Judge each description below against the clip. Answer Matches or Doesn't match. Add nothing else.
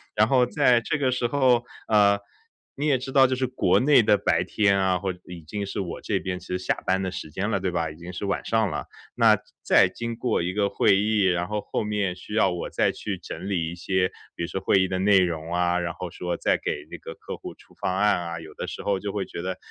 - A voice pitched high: Doesn't match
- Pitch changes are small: Doesn't match